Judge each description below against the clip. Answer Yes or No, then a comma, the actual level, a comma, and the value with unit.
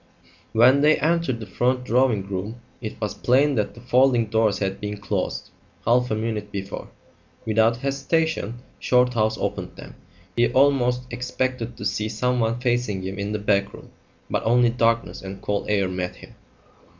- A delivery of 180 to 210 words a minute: No, average, 160 wpm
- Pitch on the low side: Yes, low, 115 Hz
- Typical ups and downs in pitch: Yes, average, 3.2 semitones